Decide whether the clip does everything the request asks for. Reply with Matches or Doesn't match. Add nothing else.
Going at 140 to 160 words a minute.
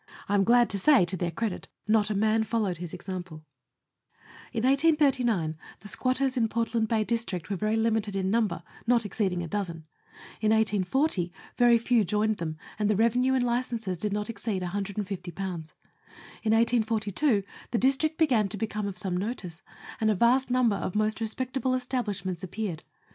Doesn't match